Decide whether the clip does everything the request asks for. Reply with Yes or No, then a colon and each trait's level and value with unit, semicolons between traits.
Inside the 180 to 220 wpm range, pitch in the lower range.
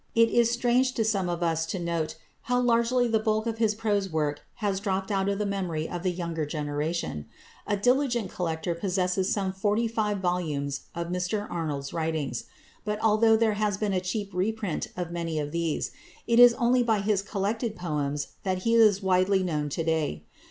No: average, 190 wpm; high, 190 Hz